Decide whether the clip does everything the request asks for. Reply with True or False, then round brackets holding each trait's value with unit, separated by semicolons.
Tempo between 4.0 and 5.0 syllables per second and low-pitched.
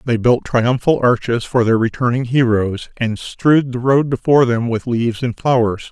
True (4.9 syllables/s; 120 Hz)